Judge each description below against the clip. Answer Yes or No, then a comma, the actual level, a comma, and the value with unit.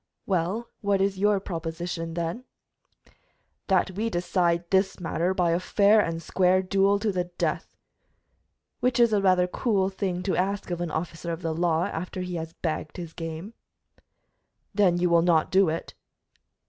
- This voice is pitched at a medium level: Yes, medium, 180 Hz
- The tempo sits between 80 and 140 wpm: No, average, 165 wpm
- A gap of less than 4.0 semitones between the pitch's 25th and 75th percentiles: Yes, average, 2.7 semitones